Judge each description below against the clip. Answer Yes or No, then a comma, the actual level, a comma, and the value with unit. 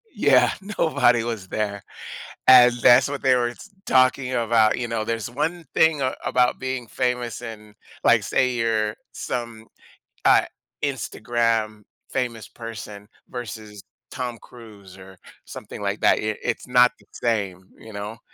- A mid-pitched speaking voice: No, low, 115 Hz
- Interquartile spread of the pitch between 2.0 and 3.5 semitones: Yes, narrow, 2.6 semitones